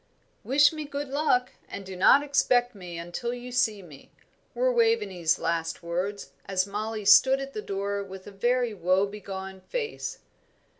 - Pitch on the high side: Yes, high, 205 Hz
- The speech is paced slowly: No, average, 160 wpm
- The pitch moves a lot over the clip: Yes, wide, 5.7 semitones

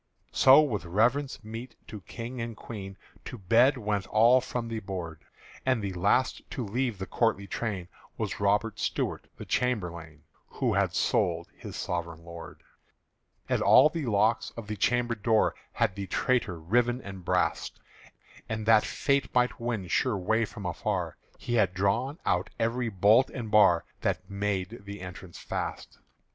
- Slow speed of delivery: No, average, 160 wpm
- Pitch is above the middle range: No, low, 110 Hz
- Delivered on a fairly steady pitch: No, average, 4.0 semitones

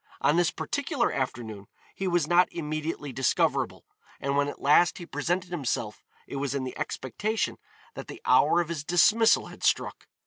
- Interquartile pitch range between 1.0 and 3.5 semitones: No, average, 4.2 semitones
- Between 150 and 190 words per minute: Yes, average, 170 wpm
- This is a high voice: No, medium, 155 Hz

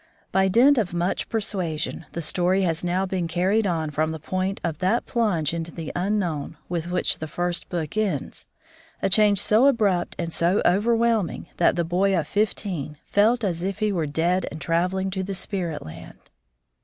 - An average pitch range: Yes, average, 3.3 semitones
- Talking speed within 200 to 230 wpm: No, average, 180 wpm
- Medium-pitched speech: Yes, medium, 180 Hz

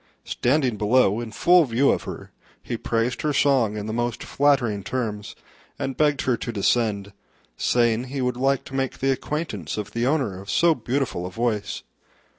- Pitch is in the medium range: No, low, 120 Hz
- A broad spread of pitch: No, average, 4.1 semitones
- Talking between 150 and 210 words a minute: Yes, average, 180 wpm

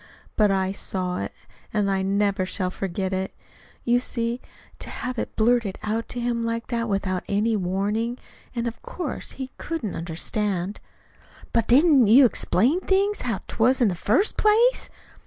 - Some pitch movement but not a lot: Yes, average, 4.1 semitones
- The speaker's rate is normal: Yes, average, 160 wpm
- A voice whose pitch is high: Yes, high, 225 Hz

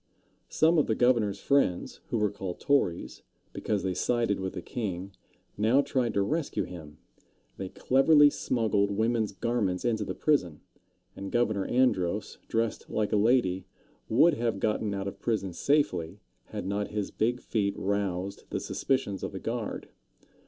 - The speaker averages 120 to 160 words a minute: Yes, average, 155 wpm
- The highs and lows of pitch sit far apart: No, average, 3.9 semitones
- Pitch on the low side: Yes, low, 105 Hz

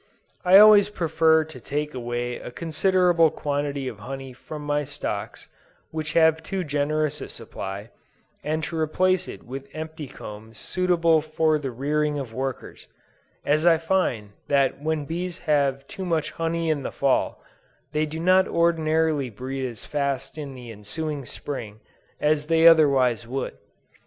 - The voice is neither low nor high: Yes, medium, 150 Hz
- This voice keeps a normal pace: Yes, average, 150 wpm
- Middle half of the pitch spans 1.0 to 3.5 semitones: Yes, average, 3.2 semitones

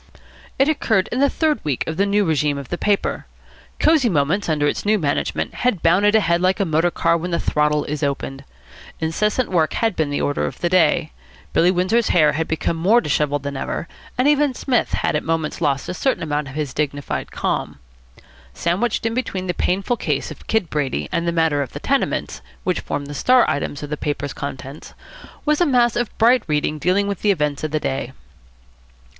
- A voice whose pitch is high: No, medium, 170 Hz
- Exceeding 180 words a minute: Yes, fast, 205 wpm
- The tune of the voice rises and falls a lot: Yes, wide, 6.1 semitones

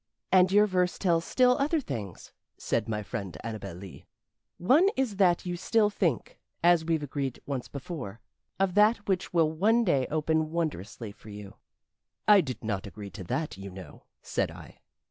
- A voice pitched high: No, medium, 160 Hz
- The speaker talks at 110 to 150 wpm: No, average, 170 wpm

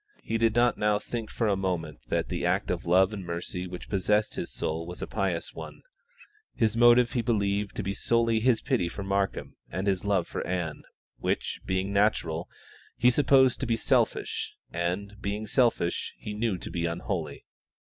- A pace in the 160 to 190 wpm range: Yes, average, 185 wpm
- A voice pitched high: No, low, 100 Hz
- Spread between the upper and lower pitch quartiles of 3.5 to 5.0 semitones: Yes, average, 4.0 semitones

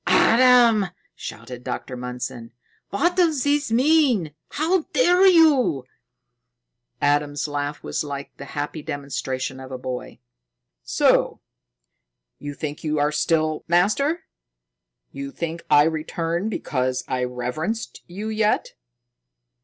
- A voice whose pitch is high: No, medium, 155 Hz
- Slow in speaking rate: Yes, slow, 115 wpm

